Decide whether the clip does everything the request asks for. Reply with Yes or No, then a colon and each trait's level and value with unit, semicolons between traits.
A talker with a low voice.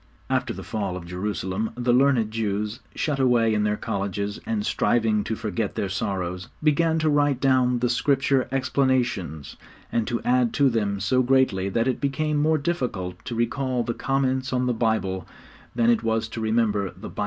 Yes: low, 115 Hz